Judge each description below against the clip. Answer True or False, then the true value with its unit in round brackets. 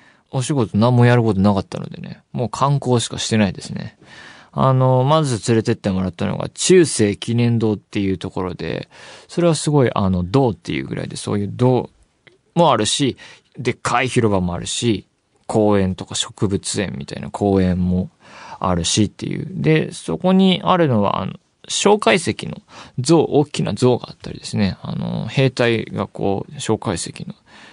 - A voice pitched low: True (115 Hz)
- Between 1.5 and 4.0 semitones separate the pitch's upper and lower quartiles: False (5.2 semitones)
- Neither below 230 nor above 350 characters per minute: True (330 characters per minute)